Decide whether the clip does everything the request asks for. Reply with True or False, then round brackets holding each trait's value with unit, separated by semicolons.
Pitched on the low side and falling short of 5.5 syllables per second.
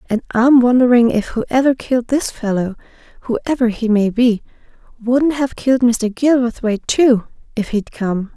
False (240 Hz; 4.7 syllables/s)